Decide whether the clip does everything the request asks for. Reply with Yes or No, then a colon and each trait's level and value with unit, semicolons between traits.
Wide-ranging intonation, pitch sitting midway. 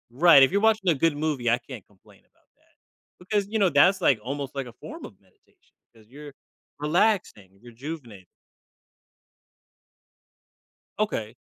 Yes: wide, 7.9 semitones; medium, 145 Hz